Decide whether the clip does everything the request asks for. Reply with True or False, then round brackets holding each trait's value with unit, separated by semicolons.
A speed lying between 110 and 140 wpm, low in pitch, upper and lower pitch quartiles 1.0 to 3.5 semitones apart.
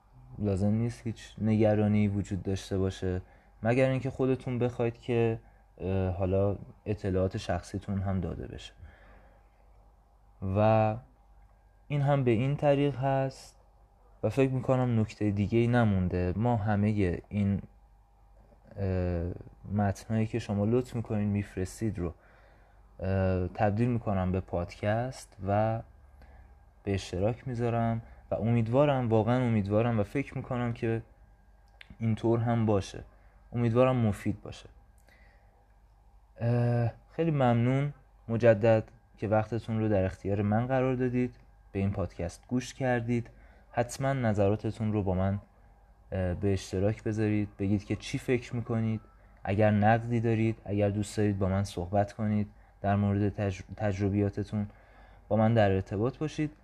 True (120 wpm; 105 Hz; 2.8 semitones)